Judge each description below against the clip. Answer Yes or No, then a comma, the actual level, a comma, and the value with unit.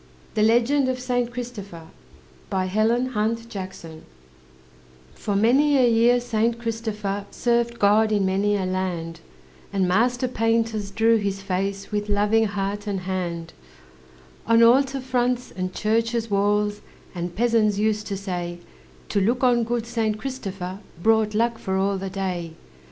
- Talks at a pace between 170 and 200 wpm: No, slow, 135 wpm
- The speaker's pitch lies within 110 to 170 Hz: No, high, 210 Hz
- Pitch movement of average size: Yes, average, 3.5 semitones